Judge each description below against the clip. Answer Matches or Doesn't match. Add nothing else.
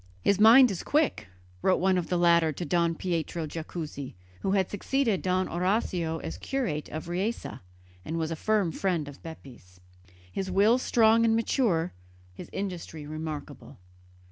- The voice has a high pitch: Doesn't match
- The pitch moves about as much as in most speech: Matches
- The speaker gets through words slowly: Doesn't match